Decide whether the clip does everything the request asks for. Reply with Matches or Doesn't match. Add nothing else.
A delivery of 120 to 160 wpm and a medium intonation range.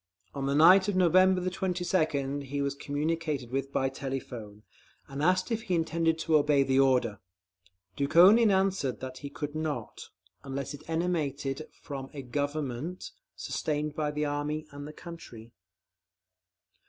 Matches